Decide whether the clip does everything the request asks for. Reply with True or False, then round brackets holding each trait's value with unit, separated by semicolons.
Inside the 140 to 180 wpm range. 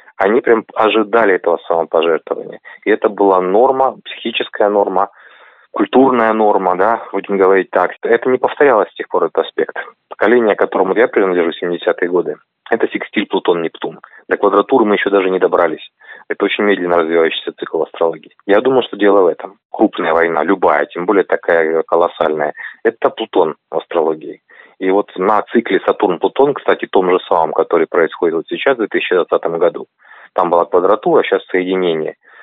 True (155 wpm)